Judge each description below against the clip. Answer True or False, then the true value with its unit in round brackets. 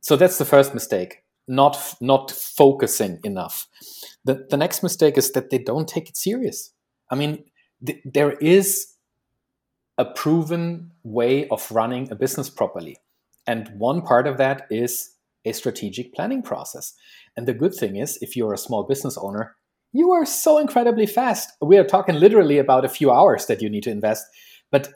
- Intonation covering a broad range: True (6.1 semitones)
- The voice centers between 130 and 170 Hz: True (140 Hz)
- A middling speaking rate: True (175 wpm)